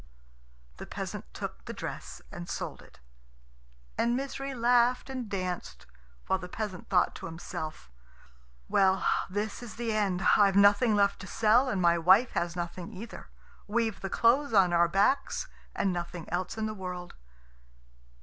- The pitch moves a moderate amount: Yes, average, 4.4 semitones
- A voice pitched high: Yes, high, 200 Hz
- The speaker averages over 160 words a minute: No, average, 155 wpm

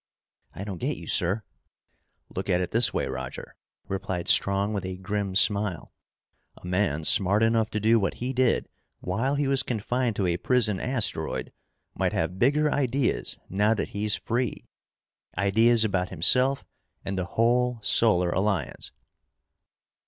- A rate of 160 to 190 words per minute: No, average, 150 wpm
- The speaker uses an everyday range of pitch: Yes, average, 4.1 semitones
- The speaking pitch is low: Yes, low, 105 Hz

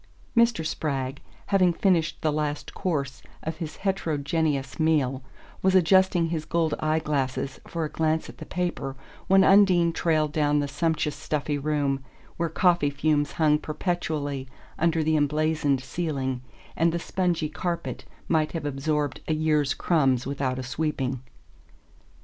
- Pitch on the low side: No, medium, 155 Hz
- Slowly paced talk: No, average, 145 wpm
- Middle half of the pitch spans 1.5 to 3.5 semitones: Yes, average, 2.8 semitones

